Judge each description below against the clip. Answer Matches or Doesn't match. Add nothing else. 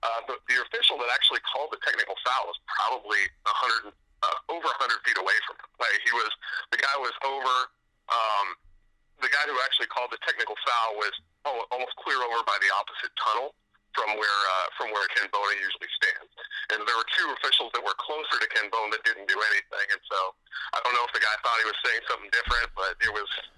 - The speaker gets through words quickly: Matches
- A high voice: Doesn't match